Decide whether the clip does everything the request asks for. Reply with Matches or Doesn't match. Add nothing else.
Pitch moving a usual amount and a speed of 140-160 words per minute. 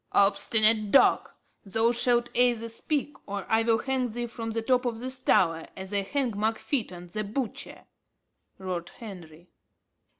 Matches